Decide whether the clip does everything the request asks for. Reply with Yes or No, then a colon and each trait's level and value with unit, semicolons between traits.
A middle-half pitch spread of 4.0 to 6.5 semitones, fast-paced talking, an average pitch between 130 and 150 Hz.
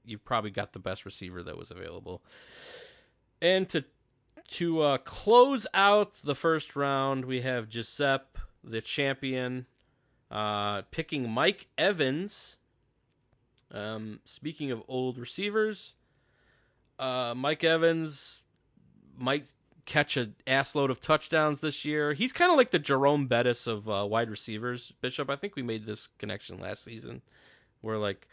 No: average, 5.2 semitones; average, 140 wpm; low, 135 Hz